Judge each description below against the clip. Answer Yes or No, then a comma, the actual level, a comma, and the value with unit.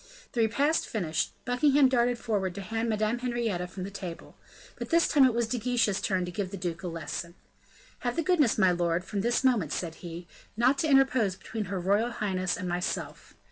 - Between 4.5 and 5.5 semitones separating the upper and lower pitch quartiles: Yes, average, 5.1 semitones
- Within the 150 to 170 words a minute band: No, fast, 205 wpm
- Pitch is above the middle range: Yes, high, 215 Hz